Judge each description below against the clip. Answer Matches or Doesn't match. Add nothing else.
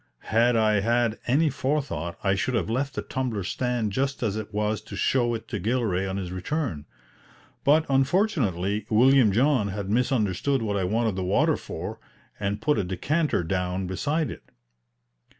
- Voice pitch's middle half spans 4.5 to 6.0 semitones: Matches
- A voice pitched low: Matches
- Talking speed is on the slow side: Doesn't match